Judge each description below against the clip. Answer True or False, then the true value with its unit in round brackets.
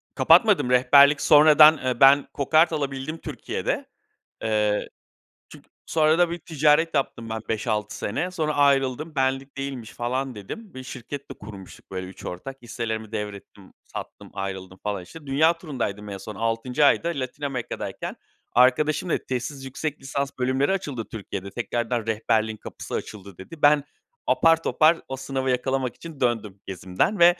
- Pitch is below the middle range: True (130 Hz)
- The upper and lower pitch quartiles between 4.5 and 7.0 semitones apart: True (5.1 semitones)